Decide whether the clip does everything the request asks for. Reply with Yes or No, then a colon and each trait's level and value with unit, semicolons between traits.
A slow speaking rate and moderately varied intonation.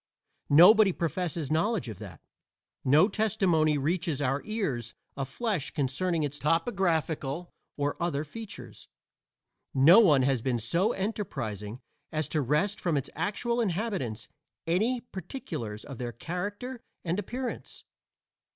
No: slow, 125 wpm; wide, 6.7 semitones